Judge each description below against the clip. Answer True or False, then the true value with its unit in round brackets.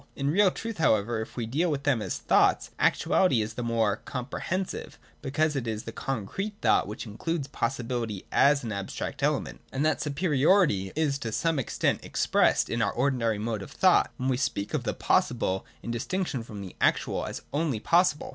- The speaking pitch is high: False (130 Hz)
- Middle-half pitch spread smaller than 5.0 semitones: False (5.6 semitones)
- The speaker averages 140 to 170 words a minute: False (185 wpm)